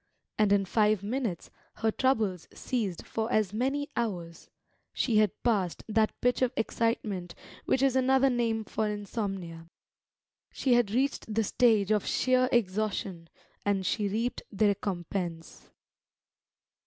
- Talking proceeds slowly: Yes, slow, 130 wpm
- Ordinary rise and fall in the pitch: Yes, average, 3.7 semitones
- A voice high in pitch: Yes, high, 215 Hz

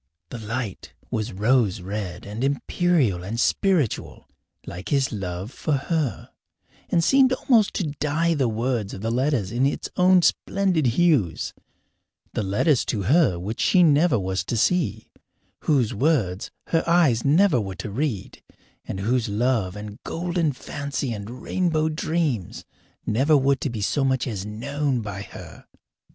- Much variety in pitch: Yes, wide, 6.9 semitones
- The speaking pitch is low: Yes, low, 130 Hz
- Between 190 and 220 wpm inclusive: No, average, 150 wpm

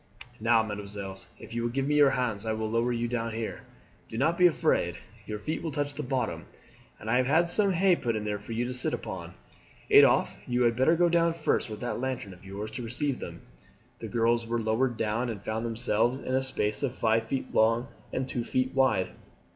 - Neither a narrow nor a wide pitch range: Yes, average, 3.2 semitones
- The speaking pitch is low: Yes, low, 120 Hz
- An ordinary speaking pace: No, fast, 220 wpm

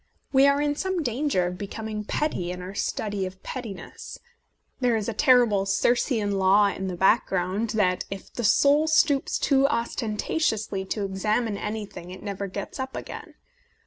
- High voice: Yes, high, 215 Hz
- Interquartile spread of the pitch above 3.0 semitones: Yes, average, 5.2 semitones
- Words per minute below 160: No, average, 170 wpm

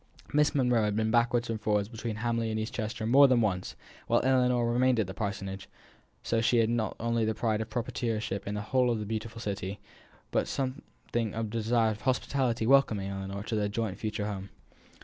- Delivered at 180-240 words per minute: Yes, fast, 205 wpm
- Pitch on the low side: Yes, low, 110 Hz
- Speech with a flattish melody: Yes, narrow, 2.3 semitones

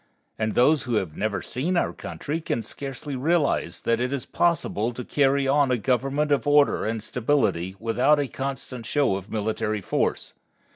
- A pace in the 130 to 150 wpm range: No, average, 175 wpm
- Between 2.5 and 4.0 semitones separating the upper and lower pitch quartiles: No, average, 4.5 semitones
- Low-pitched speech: Yes, low, 130 Hz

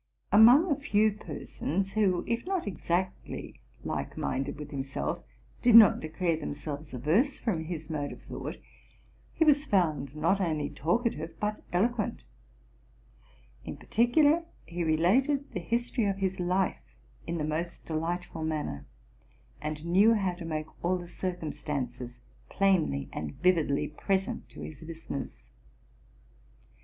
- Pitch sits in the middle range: Yes, medium, 175 Hz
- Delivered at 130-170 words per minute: Yes, slow, 135 wpm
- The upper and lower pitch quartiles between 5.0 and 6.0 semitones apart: Yes, average, 5.3 semitones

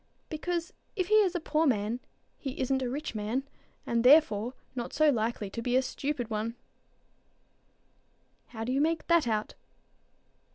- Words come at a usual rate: Yes, average, 155 wpm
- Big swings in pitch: No, average, 5.0 semitones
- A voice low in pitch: No, very high, 260 Hz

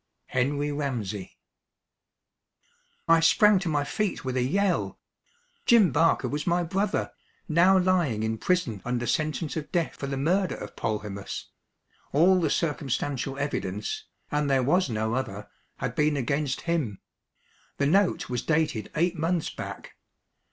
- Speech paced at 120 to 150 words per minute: Yes, average, 140 wpm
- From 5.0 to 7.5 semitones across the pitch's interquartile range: Yes, wide, 5.4 semitones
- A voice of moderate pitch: Yes, medium, 150 Hz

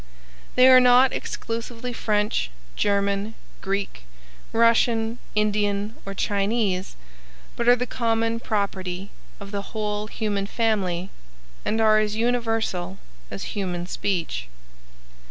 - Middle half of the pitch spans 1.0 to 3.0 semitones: Yes, narrow, 2.6 semitones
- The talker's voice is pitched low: No, high, 210 Hz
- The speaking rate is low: Yes, slow, 110 wpm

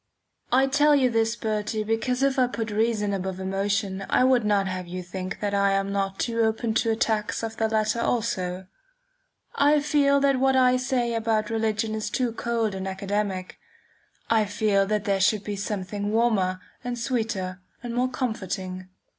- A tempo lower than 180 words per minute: Yes, average, 170 wpm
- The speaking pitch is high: Yes, high, 220 Hz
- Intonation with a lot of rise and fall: No, average, 3.3 semitones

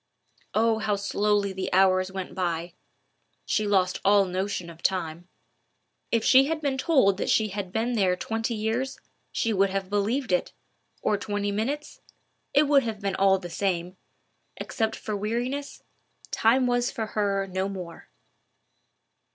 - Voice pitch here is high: Yes, high, 205 Hz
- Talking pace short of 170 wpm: Yes, average, 145 wpm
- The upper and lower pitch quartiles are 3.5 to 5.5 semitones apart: No, average, 3.1 semitones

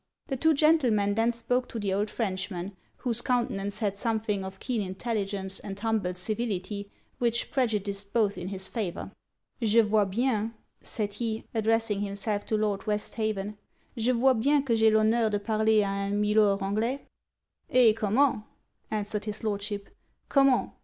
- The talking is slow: No, average, 155 wpm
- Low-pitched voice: No, high, 215 Hz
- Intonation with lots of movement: No, narrow, 2.4 semitones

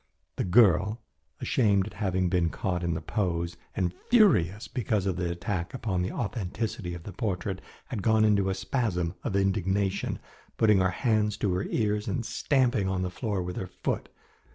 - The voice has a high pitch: No, very low, 95 Hz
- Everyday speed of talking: Yes, average, 175 wpm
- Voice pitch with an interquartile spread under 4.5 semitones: Yes, average, 3.2 semitones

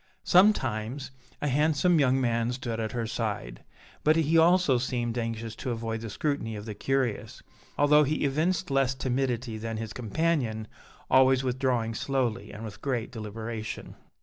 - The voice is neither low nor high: No, low, 125 Hz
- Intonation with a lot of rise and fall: No, average, 3.7 semitones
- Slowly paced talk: No, average, 150 wpm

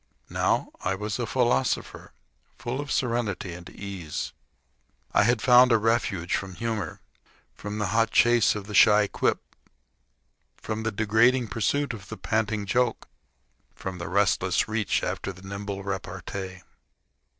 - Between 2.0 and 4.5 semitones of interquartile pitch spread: Yes, average, 3.2 semitones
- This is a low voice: Yes, low, 105 Hz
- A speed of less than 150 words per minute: Yes, average, 140 wpm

